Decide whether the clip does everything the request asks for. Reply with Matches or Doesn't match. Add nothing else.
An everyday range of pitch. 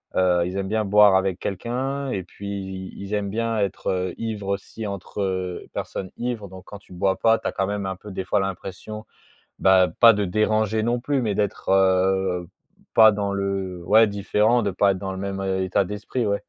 Doesn't match